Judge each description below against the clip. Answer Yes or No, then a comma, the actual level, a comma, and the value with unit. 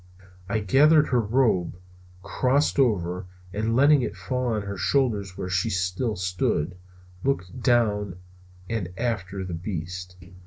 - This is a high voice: No, low, 105 Hz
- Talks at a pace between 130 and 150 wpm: Yes, average, 140 wpm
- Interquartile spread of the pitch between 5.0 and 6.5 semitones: Yes, average, 5.3 semitones